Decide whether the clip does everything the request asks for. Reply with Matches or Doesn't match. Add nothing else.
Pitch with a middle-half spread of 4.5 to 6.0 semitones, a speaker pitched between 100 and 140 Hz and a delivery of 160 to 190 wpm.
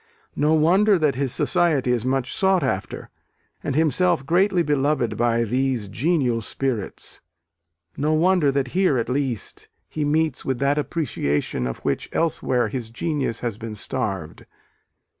Doesn't match